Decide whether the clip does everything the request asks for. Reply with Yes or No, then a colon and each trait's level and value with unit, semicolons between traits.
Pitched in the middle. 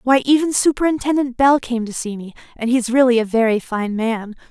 No: high, 245 Hz